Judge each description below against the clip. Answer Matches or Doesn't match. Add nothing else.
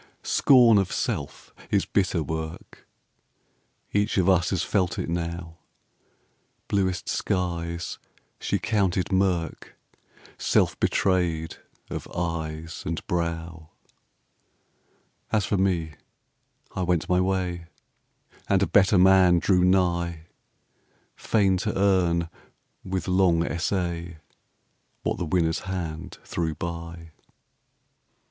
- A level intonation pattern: Matches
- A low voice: Matches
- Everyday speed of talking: Doesn't match